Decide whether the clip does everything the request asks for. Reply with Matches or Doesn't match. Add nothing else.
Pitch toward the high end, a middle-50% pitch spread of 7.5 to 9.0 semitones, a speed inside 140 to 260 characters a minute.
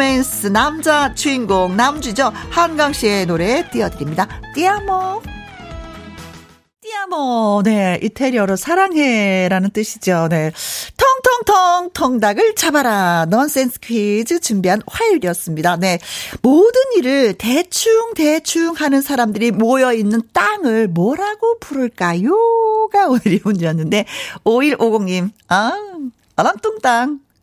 Matches